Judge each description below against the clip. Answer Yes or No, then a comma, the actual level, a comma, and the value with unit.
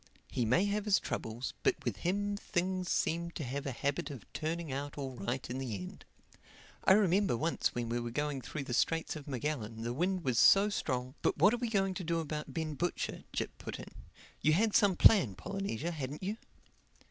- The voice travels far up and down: Yes, wide, 6.6 semitones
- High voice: No, medium, 155 Hz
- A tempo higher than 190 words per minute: Yes, fast, 205 wpm